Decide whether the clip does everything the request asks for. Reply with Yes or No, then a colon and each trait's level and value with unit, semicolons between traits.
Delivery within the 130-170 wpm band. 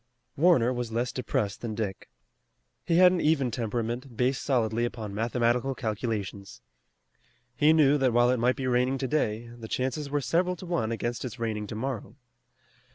Yes: average, 160 wpm